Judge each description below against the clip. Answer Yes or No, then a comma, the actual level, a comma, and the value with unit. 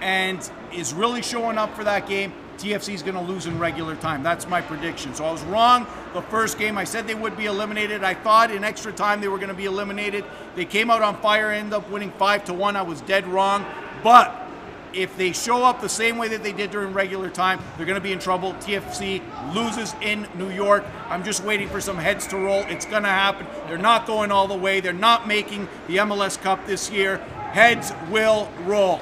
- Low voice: No, high, 200 Hz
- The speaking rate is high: Yes, fast, 230 wpm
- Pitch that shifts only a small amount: Yes, narrow, 2.1 semitones